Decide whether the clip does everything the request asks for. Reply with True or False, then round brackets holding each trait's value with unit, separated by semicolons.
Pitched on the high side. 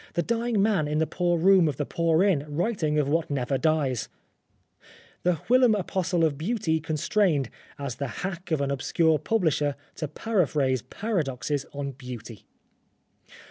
False (160 Hz)